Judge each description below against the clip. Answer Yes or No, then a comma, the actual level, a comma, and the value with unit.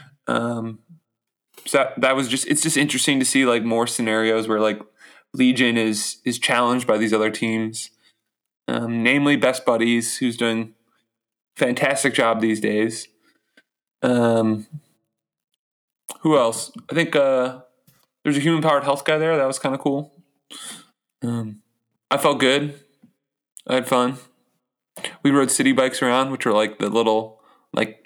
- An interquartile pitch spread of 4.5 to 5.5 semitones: No, average, 3.6 semitones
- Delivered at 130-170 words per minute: Yes, average, 150 wpm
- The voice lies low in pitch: Yes, low, 125 Hz